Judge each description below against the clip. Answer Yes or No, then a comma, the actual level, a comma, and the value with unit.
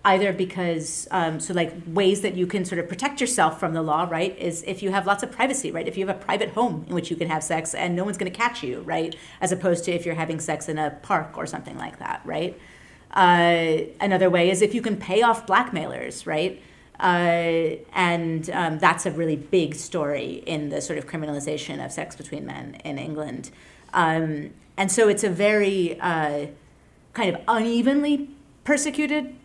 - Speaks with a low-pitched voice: No, medium, 180 Hz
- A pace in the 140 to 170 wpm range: No, fast, 205 wpm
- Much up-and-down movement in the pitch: No, average, 3.8 semitones